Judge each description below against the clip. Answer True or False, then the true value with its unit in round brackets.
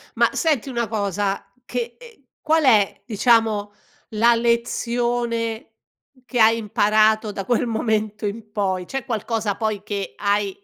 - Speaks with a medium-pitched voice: False (220 Hz)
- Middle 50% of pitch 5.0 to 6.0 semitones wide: False (2.4 semitones)